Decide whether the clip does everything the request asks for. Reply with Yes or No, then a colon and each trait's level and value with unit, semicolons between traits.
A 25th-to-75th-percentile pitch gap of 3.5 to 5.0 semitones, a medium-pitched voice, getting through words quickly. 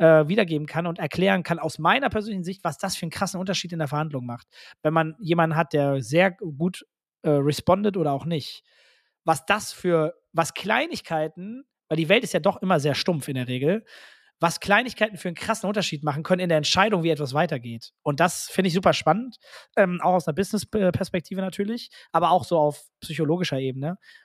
Yes: average, 3.8 semitones; medium, 170 Hz; fast, 200 wpm